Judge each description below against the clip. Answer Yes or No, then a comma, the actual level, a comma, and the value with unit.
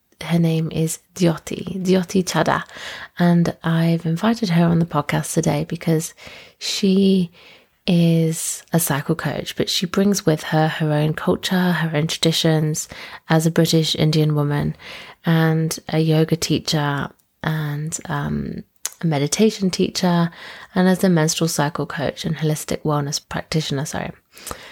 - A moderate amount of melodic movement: No, narrow, 2.2 semitones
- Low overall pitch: No, medium, 165 Hz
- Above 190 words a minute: No, slow, 135 wpm